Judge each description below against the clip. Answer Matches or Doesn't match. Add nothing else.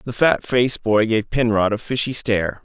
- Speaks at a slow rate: Doesn't match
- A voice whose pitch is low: Matches